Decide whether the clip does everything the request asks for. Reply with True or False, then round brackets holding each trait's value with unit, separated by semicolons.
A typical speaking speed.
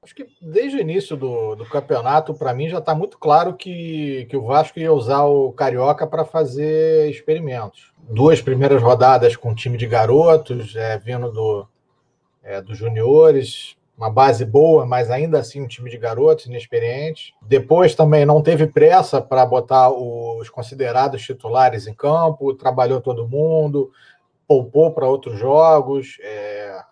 True (155 wpm)